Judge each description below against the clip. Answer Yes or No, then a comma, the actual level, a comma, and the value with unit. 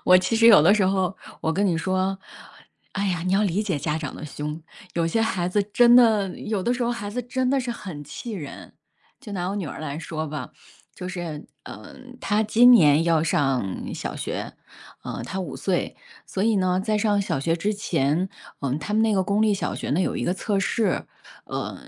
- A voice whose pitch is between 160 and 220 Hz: Yes, high, 190 Hz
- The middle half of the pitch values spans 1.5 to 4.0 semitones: No, average, 4.4 semitones